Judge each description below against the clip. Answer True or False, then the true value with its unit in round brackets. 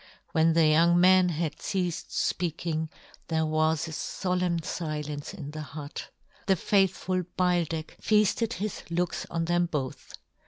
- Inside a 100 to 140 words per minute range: True (135 wpm)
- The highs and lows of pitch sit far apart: False (2.5 semitones)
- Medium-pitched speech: True (170 Hz)